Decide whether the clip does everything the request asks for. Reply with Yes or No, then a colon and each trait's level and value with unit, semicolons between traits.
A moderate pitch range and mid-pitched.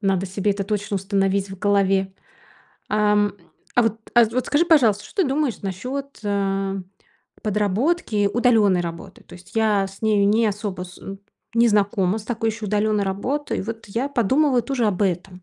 No: average, 3.0 semitones; high, 205 Hz